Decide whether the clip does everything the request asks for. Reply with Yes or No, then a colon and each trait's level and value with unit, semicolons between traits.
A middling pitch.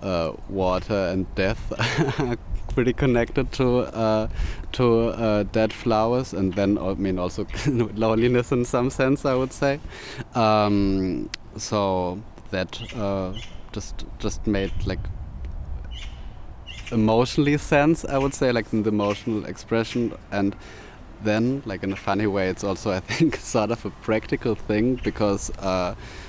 No: low, 105 Hz